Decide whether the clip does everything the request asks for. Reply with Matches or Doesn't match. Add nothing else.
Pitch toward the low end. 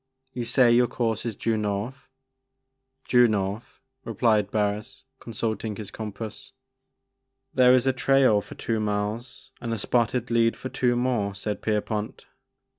Matches